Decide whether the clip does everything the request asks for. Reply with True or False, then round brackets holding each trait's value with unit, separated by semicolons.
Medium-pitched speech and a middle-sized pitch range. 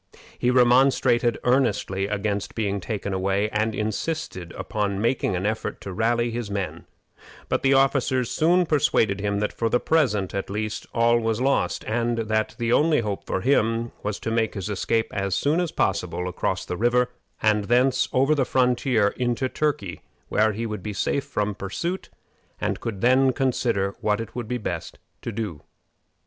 False (115 Hz; 3.7 semitones)